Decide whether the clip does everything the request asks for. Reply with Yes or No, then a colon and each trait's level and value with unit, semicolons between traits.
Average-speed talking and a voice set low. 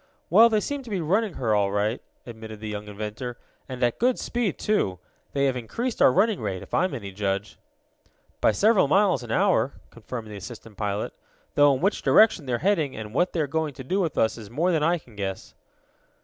No: fast, 220 wpm; low, 130 Hz